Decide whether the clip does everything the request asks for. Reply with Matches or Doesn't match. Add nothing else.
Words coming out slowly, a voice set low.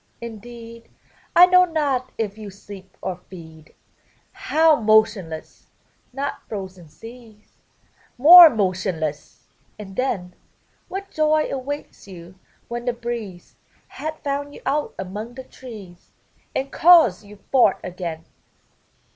Doesn't match